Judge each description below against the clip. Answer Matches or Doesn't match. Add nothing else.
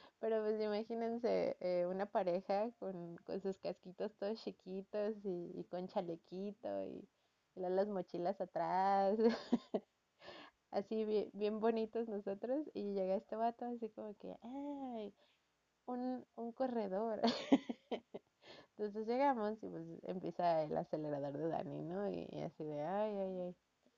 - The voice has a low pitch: Doesn't match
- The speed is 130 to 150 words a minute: Matches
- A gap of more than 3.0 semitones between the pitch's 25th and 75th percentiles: Matches